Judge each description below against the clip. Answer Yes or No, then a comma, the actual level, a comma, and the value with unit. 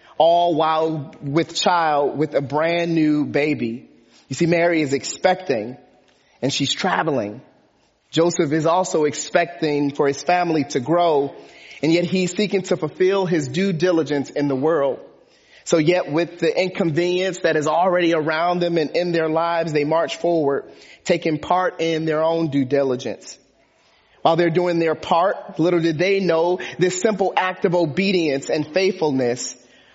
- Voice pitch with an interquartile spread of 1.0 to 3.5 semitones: Yes, average, 2.7 semitones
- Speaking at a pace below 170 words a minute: Yes, average, 155 wpm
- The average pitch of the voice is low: No, medium, 165 Hz